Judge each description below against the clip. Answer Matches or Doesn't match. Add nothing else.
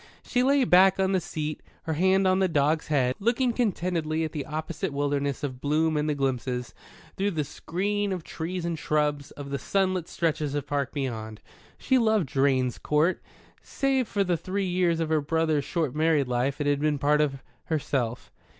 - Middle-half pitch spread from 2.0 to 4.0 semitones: Doesn't match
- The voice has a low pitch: Doesn't match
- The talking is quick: Doesn't match